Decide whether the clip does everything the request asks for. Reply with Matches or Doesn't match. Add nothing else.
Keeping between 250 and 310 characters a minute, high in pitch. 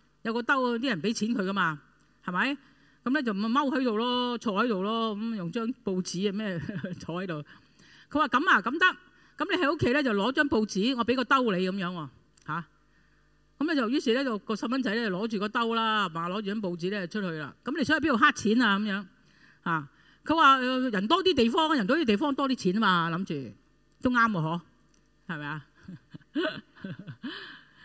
Matches